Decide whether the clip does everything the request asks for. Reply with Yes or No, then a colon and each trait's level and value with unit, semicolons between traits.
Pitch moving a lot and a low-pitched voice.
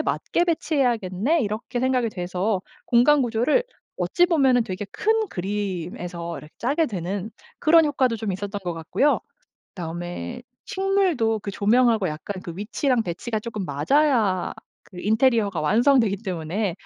No: wide, 6.0 semitones; high, 220 Hz